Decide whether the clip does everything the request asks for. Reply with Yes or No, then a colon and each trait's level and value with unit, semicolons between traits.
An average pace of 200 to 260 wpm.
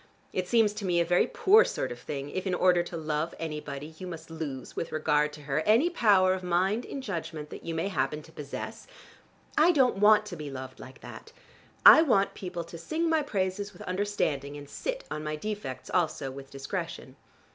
Yes: fast, 205 wpm